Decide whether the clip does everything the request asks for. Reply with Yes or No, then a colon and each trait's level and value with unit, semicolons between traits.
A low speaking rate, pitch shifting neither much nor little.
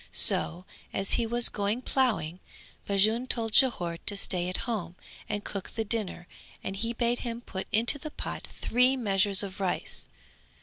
No: average, 165 wpm; average, 3.8 semitones